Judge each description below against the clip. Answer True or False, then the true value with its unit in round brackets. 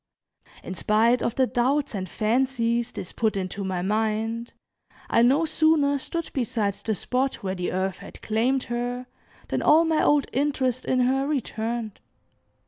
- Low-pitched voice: False (240 Hz)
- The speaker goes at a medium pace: True (155 wpm)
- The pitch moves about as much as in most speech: True (3.8 semitones)